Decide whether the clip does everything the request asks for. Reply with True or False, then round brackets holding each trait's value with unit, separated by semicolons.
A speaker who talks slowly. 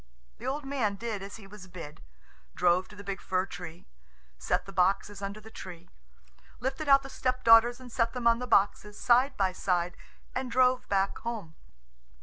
False (180 wpm)